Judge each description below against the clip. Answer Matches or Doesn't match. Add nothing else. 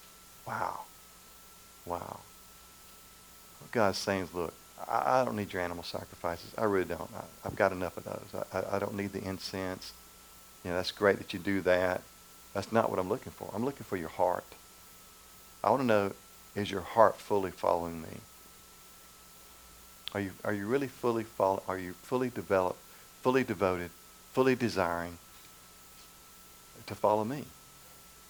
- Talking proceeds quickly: Doesn't match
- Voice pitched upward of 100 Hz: Doesn't match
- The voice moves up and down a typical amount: Doesn't match